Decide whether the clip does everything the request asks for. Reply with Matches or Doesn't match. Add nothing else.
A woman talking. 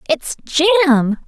Matches